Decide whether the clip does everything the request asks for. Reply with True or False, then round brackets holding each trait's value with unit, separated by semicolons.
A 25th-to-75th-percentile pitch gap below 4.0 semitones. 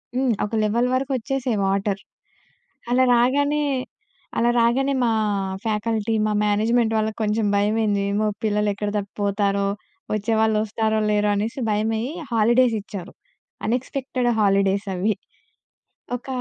True (2.6 semitones)